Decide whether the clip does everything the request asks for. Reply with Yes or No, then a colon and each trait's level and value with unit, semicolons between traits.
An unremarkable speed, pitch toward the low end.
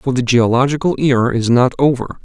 Yes: average, 190 wpm; low, 130 Hz